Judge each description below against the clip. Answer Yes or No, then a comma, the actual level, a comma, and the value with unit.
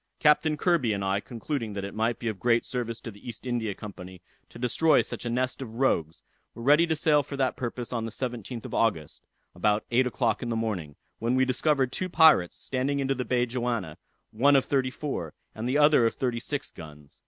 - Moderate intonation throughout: Yes, average, 3.6 semitones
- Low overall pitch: Yes, low, 120 Hz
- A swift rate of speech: Yes, fast, 220 wpm